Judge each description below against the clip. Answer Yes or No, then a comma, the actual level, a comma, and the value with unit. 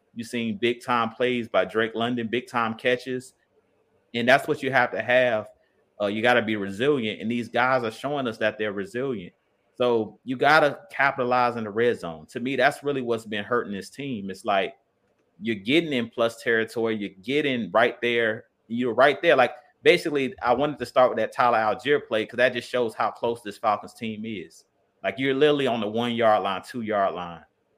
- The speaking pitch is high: No, low, 120 Hz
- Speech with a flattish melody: Yes, narrow, 2.3 semitones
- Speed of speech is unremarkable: No, fast, 210 wpm